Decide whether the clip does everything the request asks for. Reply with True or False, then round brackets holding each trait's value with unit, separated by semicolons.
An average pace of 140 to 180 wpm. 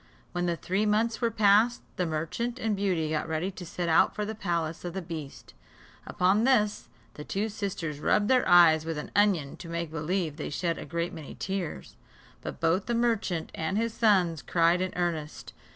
False (195 wpm)